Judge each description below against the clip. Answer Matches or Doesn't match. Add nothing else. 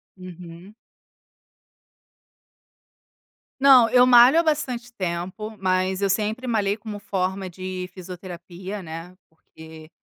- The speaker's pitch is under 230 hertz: Matches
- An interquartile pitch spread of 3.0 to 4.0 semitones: Matches